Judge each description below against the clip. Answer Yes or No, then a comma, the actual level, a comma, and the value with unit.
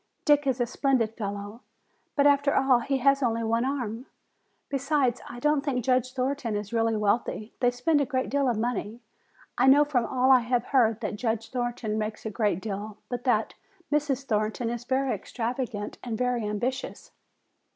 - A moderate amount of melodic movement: Yes, average, 3.2 semitones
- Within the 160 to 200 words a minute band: Yes, average, 180 wpm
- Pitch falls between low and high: No, high, 245 Hz